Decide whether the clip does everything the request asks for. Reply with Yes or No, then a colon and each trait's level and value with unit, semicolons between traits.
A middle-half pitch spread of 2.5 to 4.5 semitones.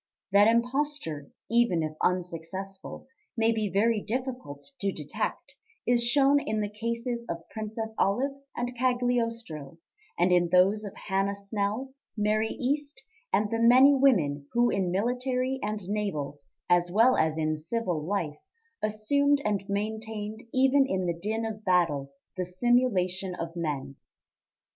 No: average, 5.1 semitones